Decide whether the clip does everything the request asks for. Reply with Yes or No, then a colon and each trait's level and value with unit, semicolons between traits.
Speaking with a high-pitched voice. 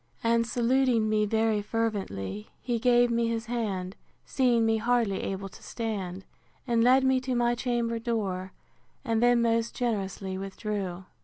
Yes: high, 230 Hz